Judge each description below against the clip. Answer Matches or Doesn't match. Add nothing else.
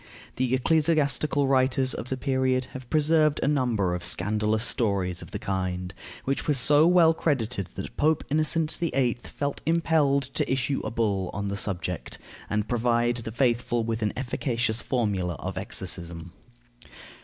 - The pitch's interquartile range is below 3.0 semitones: Doesn't match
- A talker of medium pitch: Doesn't match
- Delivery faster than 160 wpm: Doesn't match